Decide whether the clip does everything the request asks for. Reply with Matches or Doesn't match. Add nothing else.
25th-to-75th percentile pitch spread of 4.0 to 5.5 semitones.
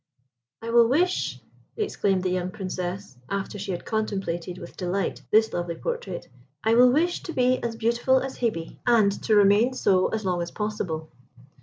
Matches